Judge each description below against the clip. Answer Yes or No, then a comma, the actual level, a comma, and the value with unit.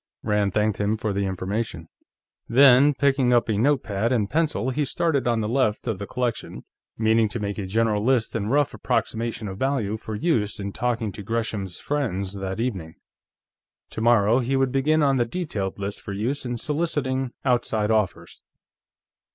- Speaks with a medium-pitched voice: No, low, 115 Hz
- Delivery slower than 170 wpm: No, average, 175 wpm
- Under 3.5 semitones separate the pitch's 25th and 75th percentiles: No, average, 4.2 semitones